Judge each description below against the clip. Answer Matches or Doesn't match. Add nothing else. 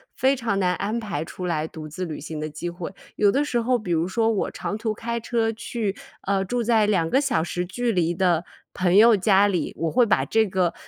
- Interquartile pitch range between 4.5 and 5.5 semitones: Matches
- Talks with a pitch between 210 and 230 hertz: Doesn't match